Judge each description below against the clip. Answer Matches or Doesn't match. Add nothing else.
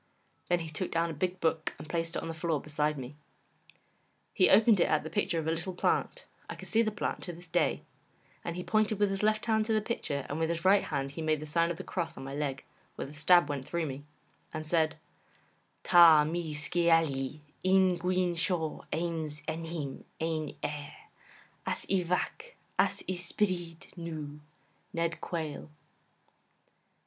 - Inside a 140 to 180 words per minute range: Doesn't match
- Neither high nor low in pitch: Matches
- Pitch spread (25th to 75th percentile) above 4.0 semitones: Doesn't match